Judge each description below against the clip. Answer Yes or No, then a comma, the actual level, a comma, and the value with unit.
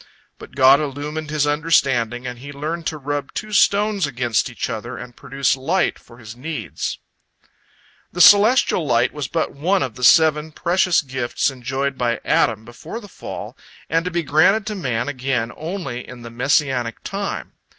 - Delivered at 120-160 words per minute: No, average, 170 wpm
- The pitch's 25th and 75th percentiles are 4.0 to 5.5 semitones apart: Yes, average, 4.9 semitones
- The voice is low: No, medium, 145 Hz